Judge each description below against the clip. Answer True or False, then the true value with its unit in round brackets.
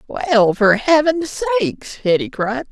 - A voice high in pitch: True (240 Hz)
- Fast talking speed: False (135 wpm)